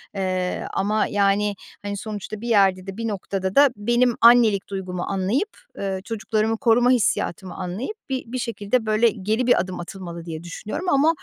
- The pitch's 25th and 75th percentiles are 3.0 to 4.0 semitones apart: Yes, average, 3.7 semitones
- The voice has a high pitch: Yes, high, 210 Hz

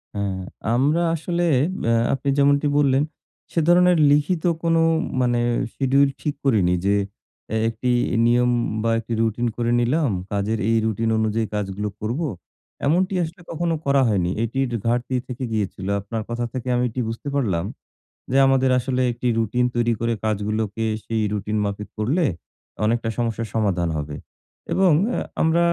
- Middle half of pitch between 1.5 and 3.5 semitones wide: No, average, 4.5 semitones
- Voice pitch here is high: No, low, 120 Hz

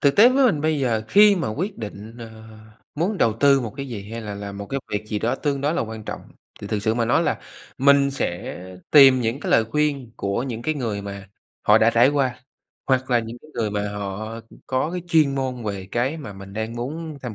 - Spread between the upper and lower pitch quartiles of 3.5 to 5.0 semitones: Yes, average, 4.6 semitones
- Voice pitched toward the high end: No, low, 120 Hz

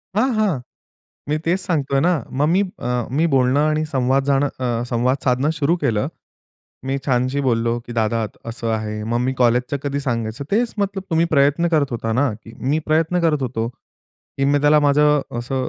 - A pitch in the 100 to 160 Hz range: Yes, low, 135 Hz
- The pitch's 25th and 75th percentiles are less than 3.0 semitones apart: No, average, 4.0 semitones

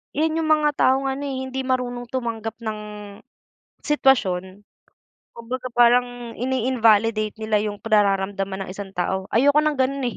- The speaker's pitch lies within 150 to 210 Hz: No, high, 240 Hz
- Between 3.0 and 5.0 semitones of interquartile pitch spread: Yes, average, 3.8 semitones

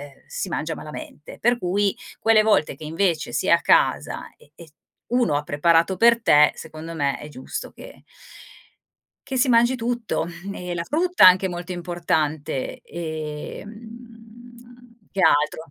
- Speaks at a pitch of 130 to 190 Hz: Yes, medium, 185 Hz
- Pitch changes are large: Yes, wide, 6.8 semitones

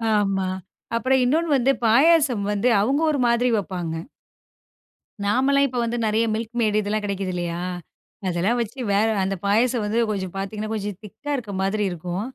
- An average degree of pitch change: Yes, average, 4.0 semitones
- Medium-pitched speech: No, high, 215 Hz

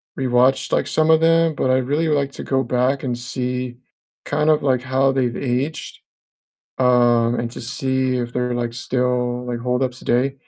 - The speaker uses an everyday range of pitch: No, narrow, 1.7 semitones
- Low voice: Yes, low, 130 Hz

